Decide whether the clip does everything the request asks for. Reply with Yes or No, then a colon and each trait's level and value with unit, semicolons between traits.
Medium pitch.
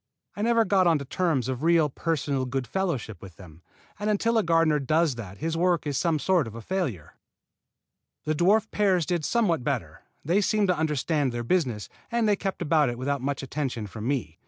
Yes: medium, 155 Hz